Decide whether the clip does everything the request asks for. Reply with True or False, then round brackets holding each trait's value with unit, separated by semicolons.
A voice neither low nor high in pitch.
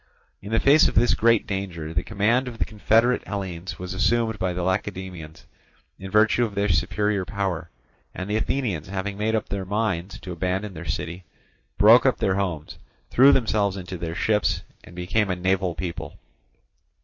False (95 Hz)